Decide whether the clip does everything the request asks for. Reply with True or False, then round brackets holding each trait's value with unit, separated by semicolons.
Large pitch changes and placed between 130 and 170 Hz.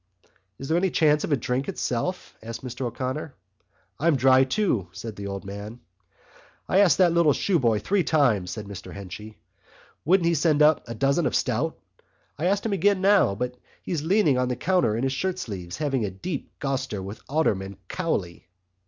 True (7.5 semitones; 135 Hz)